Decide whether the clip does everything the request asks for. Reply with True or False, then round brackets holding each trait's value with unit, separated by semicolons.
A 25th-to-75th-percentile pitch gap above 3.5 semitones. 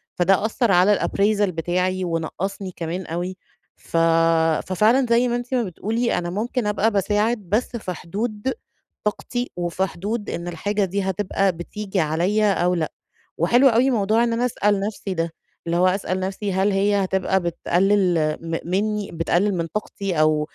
False (3.2 semitones)